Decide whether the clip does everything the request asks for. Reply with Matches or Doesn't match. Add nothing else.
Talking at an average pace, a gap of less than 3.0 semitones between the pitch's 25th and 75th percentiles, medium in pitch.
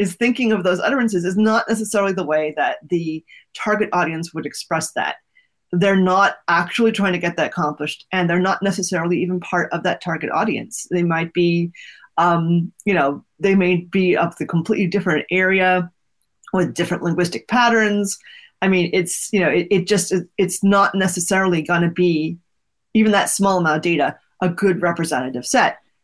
Matches